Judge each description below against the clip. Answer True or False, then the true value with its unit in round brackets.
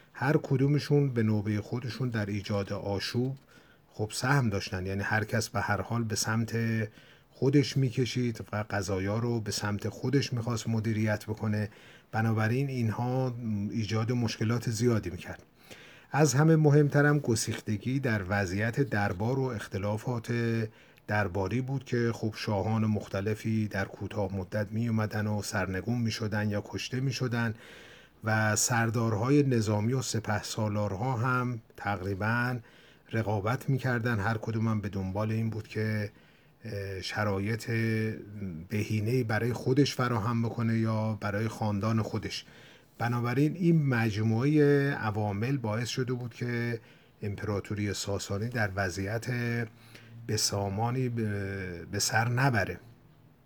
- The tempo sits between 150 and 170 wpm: False (115 wpm)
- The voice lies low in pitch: True (115 Hz)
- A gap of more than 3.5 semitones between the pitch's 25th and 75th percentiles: False (2.7 semitones)